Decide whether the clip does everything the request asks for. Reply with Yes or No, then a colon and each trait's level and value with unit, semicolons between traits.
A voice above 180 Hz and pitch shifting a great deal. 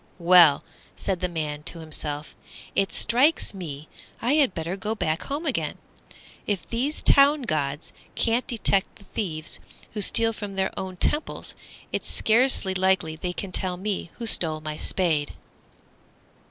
Yes: high, 190 Hz; wide, 6.1 semitones